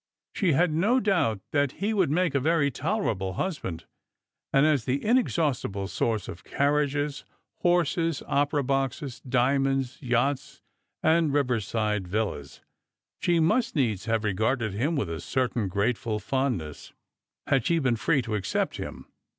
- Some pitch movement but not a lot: No, wide, 6.0 semitones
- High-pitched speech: No, low, 135 Hz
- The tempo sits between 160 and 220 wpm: No, average, 140 wpm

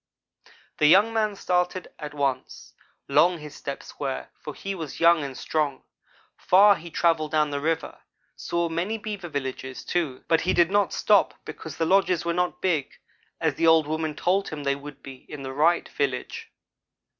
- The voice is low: No, medium, 160 Hz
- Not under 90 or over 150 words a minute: No, average, 180 wpm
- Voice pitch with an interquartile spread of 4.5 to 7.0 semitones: No, average, 3.6 semitones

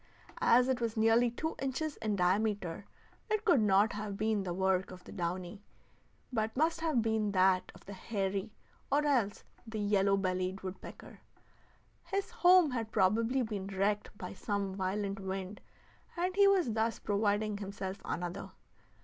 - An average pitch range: Yes, average, 3.5 semitones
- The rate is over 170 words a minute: No, average, 155 wpm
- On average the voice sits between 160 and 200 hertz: No, high, 210 Hz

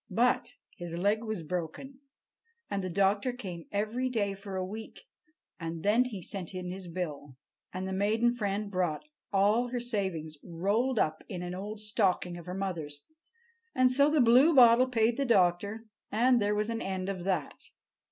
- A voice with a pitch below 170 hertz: No, high, 200 Hz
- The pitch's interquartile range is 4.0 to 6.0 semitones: Yes, average, 4.3 semitones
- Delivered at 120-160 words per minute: No, average, 170 wpm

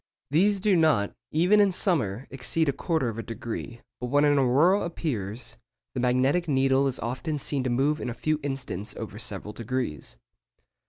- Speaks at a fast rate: No, average, 175 wpm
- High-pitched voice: No, low, 135 Hz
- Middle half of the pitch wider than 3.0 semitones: Yes, average, 4.8 semitones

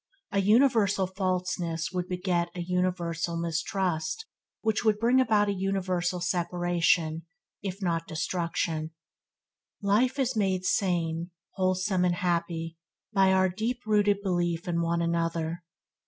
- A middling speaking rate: No, slow, 125 wpm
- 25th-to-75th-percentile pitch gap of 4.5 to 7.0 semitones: No, average, 2.8 semitones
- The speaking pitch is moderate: Yes, medium, 180 Hz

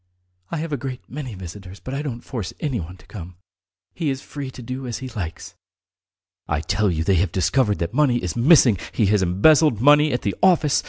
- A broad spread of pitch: Yes, wide, 6.9 semitones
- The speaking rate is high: Yes, fast, 210 wpm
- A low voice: Yes, low, 120 Hz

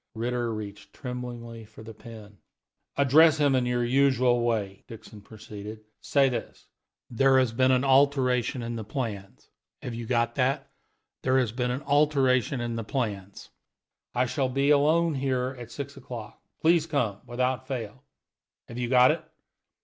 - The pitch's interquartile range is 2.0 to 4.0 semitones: Yes, average, 2.8 semitones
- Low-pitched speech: Yes, low, 125 Hz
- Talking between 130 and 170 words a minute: Yes, average, 155 wpm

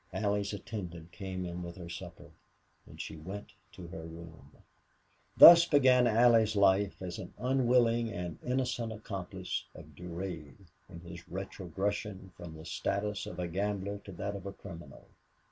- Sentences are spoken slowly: No, average, 155 wpm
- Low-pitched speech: Yes, very low, 95 Hz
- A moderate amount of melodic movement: Yes, average, 3.4 semitones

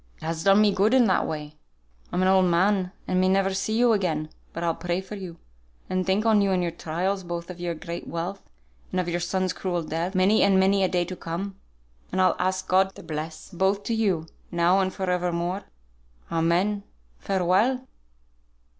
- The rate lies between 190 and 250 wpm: Yes, average, 200 wpm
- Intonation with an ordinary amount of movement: No, narrow, 2.2 semitones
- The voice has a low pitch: No, medium, 185 Hz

